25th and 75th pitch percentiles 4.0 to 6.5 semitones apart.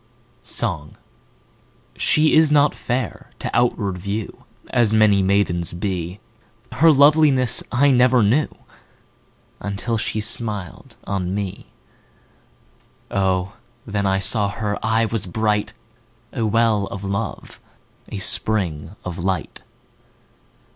No: average, 3.4 semitones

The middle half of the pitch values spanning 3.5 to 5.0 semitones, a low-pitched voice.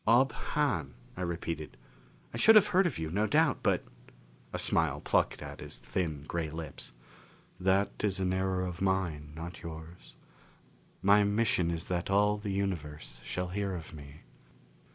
Yes: average, 4.2 semitones; very low, 90 Hz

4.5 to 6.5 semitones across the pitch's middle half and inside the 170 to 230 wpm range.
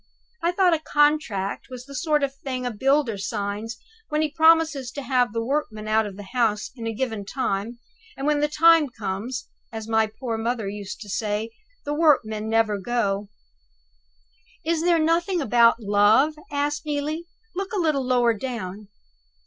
Yes: wide, 5.6 semitones; average, 175 wpm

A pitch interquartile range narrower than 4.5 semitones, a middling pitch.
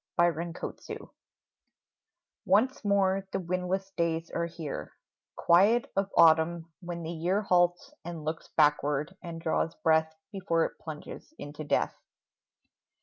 Yes: average, 2.8 semitones; medium, 170 Hz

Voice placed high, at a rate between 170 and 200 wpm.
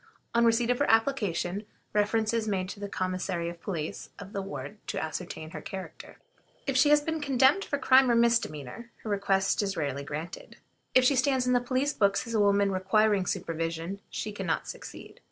Yes: high, 205 Hz; average, 195 wpm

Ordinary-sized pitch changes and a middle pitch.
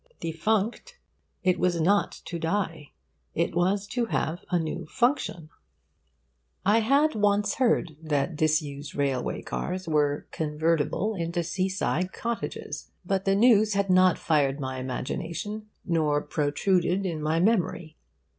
Yes: average, 4.7 semitones; medium, 175 Hz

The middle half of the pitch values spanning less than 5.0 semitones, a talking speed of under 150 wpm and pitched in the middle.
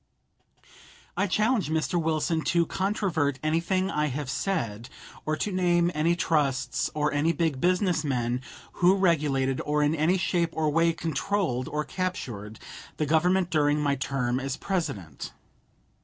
Yes: average, 4.1 semitones; average, 140 wpm; medium, 155 Hz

